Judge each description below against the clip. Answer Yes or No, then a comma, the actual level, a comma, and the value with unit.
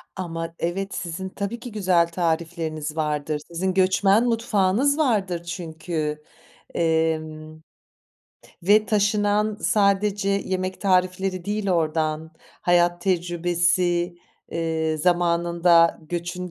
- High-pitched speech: No, medium, 175 Hz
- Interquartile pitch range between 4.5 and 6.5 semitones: No, average, 2.8 semitones